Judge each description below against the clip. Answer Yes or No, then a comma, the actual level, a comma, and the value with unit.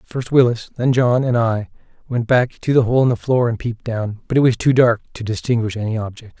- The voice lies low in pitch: Yes, low, 120 Hz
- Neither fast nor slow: No, fast, 245 wpm